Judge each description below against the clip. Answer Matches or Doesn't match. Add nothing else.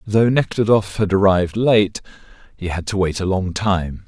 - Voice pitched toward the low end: Matches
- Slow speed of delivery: Doesn't match